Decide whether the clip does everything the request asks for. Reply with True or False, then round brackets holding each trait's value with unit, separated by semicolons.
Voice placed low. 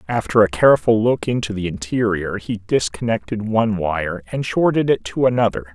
True (105 Hz)